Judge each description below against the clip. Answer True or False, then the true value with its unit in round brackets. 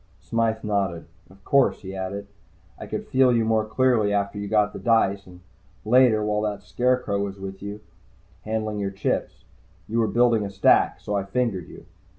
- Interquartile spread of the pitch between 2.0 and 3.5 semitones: True (2.5 semitones)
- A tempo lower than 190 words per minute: True (180 wpm)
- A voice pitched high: False (105 Hz)